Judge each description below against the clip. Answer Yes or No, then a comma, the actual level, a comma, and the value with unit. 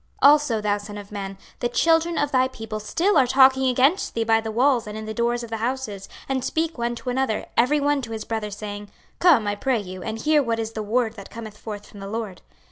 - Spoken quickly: Yes, fast, 250 wpm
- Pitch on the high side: Yes, high, 230 Hz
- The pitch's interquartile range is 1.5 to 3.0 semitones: No, average, 3.8 semitones